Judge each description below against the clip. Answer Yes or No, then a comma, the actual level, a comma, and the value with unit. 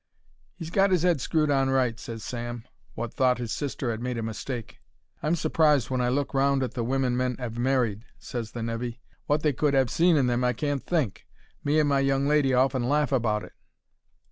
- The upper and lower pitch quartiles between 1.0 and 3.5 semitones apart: Yes, average, 3.2 semitones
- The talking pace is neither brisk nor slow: No, fast, 215 wpm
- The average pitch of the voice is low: Yes, low, 130 Hz